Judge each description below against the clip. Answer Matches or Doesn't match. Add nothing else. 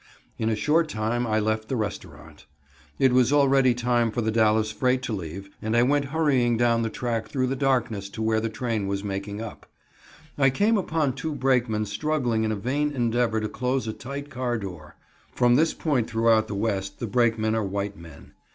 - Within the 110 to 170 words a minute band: Doesn't match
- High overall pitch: Doesn't match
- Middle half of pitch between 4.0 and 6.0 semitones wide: Doesn't match